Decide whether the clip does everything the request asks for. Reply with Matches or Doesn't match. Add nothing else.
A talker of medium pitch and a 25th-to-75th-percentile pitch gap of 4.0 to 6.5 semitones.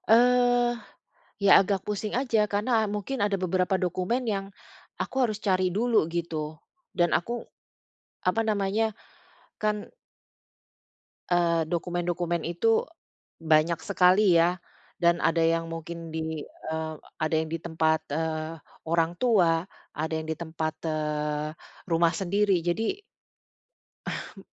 Matches